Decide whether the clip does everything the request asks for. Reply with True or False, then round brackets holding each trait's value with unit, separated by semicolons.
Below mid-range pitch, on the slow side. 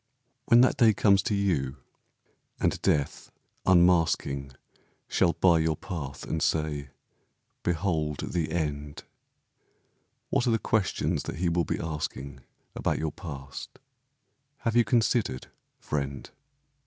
True (80 Hz; 120 wpm)